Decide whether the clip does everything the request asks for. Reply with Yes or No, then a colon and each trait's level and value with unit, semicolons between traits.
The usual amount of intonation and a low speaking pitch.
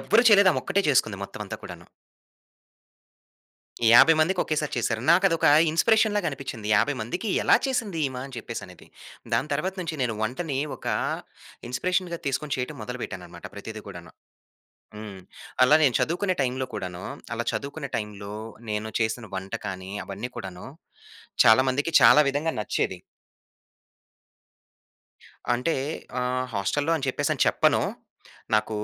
No: wide, 7.3 semitones; low, 130 Hz